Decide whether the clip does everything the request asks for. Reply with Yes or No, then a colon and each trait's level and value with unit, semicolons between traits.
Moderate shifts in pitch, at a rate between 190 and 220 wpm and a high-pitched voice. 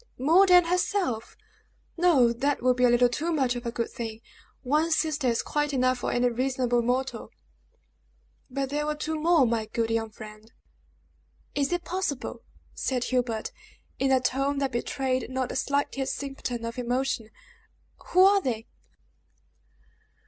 No: average, 3.7 semitones; average, 155 wpm; very high, 260 Hz